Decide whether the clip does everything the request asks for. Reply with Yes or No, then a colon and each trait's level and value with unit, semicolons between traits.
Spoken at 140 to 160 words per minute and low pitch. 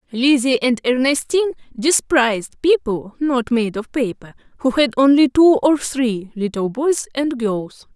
No: average, 145 wpm; very high, 255 Hz